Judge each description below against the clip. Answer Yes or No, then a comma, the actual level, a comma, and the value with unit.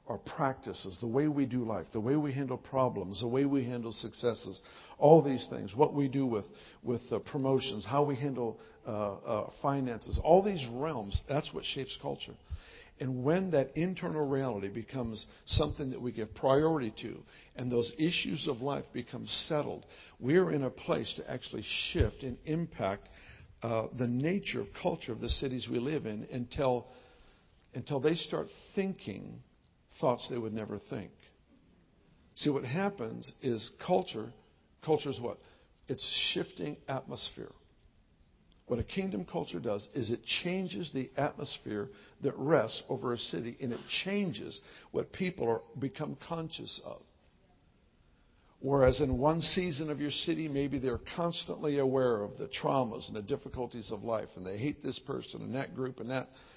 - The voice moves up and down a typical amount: Yes, average, 4.3 semitones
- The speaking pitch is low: Yes, low, 130 Hz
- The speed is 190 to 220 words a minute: No, average, 160 wpm